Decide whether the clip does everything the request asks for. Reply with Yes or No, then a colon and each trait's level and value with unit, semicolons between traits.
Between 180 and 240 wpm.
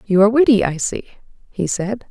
Yes: average, 200 wpm